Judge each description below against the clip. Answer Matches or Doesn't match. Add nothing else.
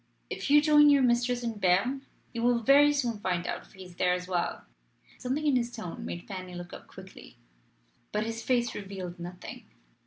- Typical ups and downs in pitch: Doesn't match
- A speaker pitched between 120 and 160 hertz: Doesn't match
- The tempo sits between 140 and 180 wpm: Doesn't match